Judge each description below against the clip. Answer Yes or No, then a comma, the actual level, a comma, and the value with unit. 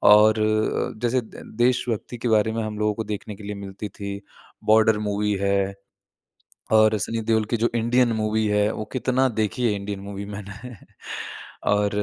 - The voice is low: Yes, low, 110 Hz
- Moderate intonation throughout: No, narrow, 1.8 semitones